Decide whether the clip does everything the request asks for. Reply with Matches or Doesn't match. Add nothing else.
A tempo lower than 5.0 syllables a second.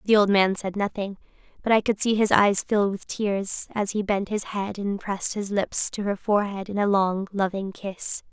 Matches